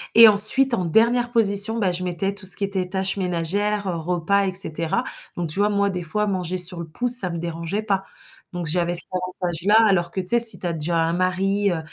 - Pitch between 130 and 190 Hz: Yes, medium, 185 Hz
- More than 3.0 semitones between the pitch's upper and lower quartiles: No, average, 2.7 semitones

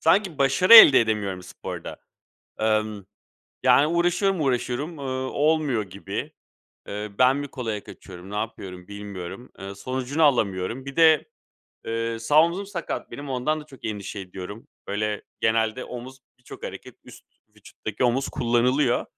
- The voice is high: No, low, 125 Hz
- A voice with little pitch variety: No, wide, 5.5 semitones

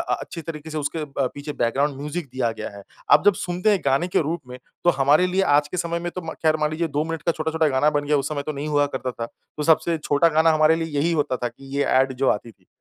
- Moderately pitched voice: Yes, medium, 150 Hz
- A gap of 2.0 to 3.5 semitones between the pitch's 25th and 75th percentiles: Yes, average, 2.8 semitones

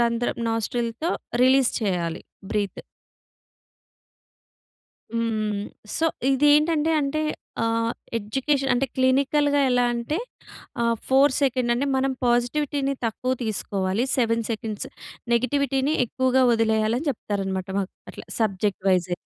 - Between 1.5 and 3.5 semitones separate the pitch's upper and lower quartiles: No, average, 3.9 semitones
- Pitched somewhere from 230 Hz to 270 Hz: Yes, high, 240 Hz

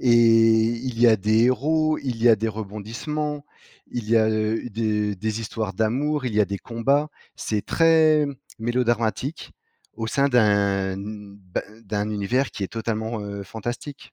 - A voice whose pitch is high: No, low, 115 Hz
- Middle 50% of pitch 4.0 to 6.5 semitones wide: No, average, 3.1 semitones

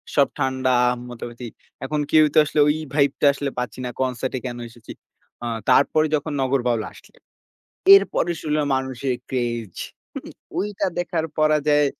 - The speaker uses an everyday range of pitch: Yes, average, 3.4 semitones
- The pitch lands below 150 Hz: Yes, low, 135 Hz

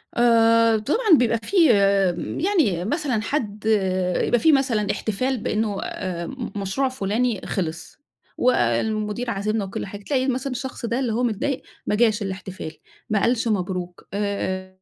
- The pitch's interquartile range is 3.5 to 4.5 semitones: Yes, average, 4.1 semitones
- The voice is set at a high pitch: Yes, high, 220 Hz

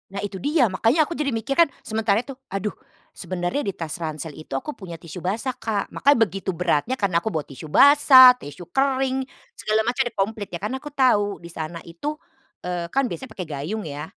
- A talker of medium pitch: No, high, 205 Hz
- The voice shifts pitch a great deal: Yes, wide, 7.2 semitones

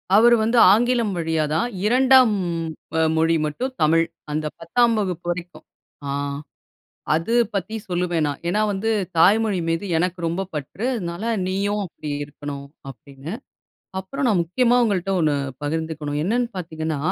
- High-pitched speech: No, medium, 180 Hz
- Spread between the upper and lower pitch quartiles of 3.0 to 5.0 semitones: No, wide, 5.5 semitones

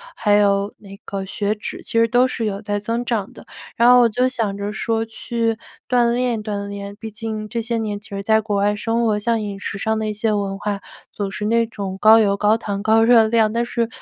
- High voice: Yes, high, 215 Hz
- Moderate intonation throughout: No, narrow, 2.1 semitones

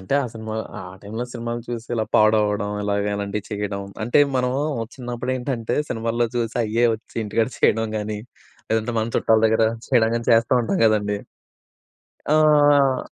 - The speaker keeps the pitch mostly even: Yes, narrow, 2.2 semitones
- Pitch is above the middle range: No, low, 115 Hz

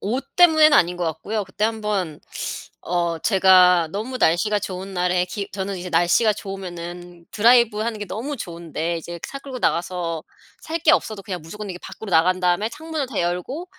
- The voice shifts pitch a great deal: No, average, 4.0 semitones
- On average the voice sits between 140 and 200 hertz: Yes, high, 190 Hz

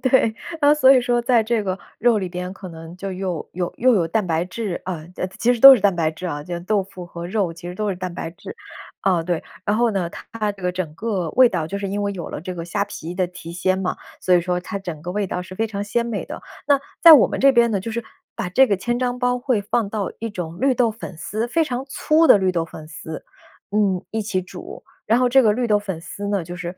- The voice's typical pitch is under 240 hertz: Yes, high, 195 Hz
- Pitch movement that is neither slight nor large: Yes, average, 4.6 semitones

